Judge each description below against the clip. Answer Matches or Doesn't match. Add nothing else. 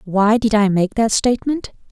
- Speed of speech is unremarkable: Matches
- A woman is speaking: Matches